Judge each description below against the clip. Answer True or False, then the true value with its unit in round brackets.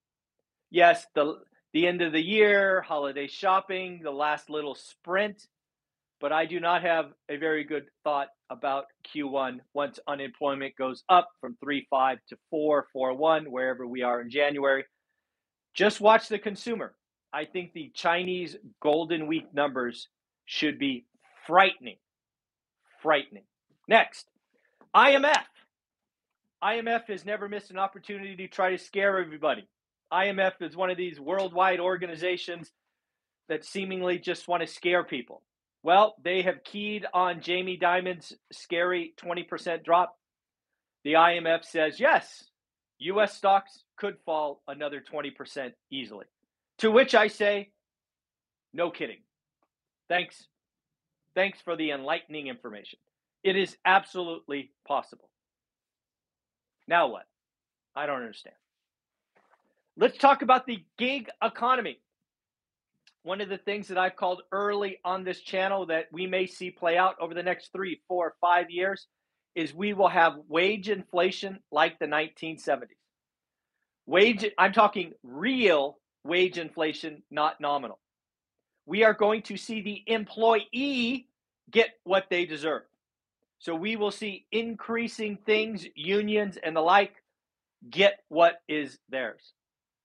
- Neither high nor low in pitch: True (180 Hz)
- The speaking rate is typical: False (130 wpm)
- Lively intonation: False (4.5 semitones)